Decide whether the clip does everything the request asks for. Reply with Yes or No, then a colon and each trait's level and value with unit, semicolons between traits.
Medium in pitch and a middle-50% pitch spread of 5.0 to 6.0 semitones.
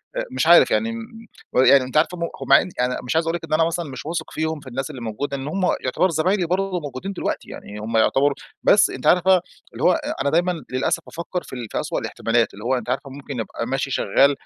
Yes: medium, 150 Hz; wide, 5.4 semitones